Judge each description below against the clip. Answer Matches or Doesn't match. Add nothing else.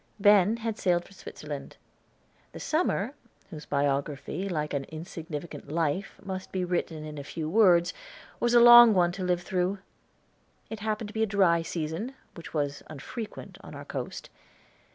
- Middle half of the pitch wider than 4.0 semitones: Matches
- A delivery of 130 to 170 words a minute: Matches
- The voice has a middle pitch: Matches